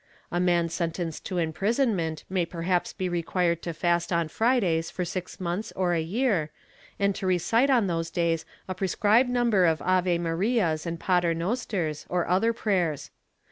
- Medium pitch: Yes, medium, 180 Hz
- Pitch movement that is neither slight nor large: Yes, average, 3.0 semitones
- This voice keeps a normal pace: Yes, average, 160 wpm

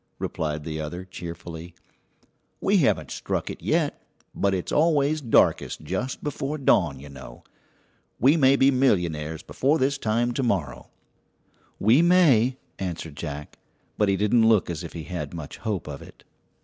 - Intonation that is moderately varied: No, wide, 8.7 semitones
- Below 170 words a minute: Yes, average, 155 wpm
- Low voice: Yes, low, 100 Hz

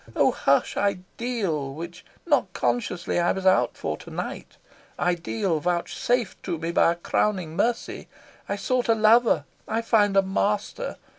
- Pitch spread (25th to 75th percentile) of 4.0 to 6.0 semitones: Yes, average, 4.6 semitones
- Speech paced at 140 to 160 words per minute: Yes, average, 150 wpm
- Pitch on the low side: No, high, 195 Hz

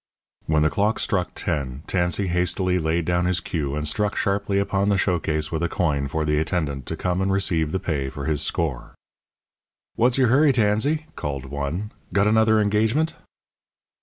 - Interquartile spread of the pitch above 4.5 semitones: Yes, average, 5.0 semitones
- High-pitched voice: No, very low, 90 Hz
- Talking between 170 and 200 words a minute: Yes, average, 180 wpm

